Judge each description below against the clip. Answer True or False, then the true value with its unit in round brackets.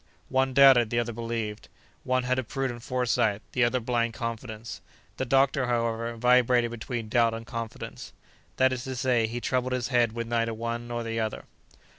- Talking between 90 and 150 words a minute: False (180 wpm)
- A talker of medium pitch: False (120 Hz)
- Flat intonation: True (1.7 semitones)